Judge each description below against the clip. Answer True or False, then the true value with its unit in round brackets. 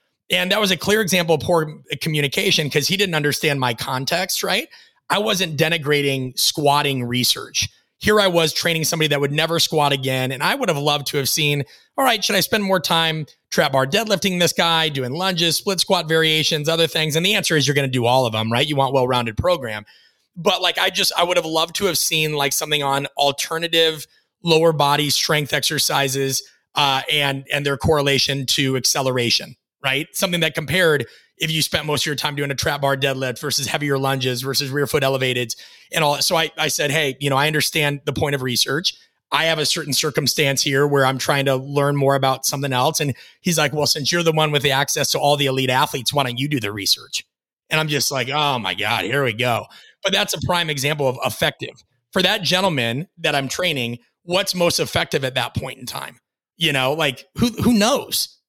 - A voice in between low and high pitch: True (145 Hz)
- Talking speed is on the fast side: True (215 wpm)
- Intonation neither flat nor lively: True (3.4 semitones)